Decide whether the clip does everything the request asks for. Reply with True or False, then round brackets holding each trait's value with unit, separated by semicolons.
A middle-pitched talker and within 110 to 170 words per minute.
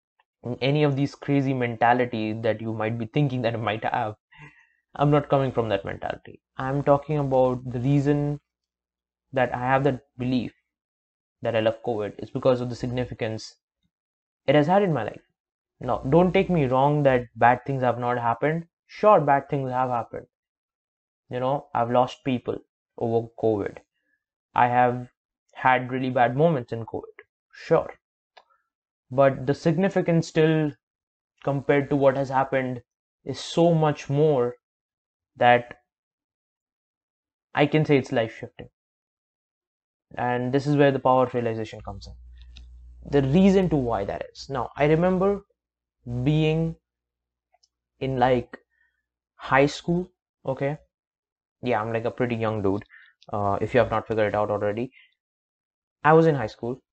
False (125 Hz; 150 wpm)